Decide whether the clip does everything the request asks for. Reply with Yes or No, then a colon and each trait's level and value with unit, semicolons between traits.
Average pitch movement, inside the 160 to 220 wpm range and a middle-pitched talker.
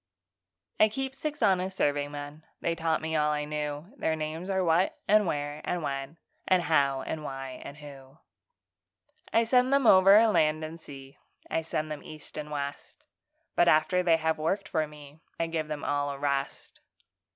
Yes: average, 3.8 semitones; average, 185 wpm; medium, 155 Hz